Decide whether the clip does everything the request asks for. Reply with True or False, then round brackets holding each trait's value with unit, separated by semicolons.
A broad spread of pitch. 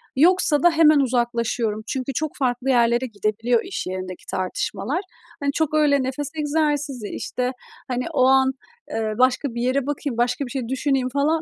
False (3.4 semitones)